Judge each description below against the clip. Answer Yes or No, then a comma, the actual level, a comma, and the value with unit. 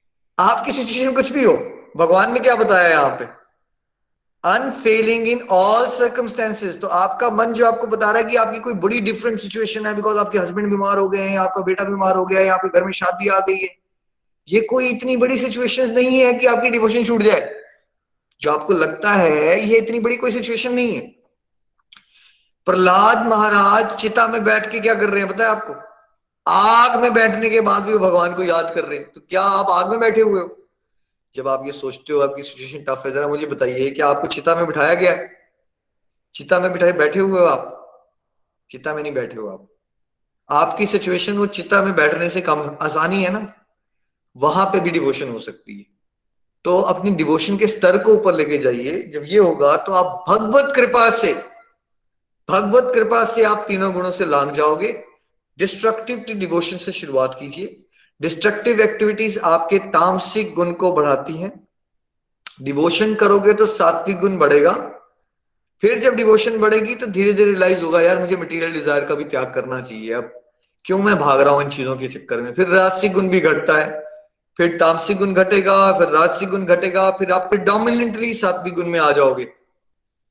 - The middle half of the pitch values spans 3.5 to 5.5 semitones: Yes, average, 4.7 semitones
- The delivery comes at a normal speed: Yes, average, 165 wpm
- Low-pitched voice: No, high, 195 Hz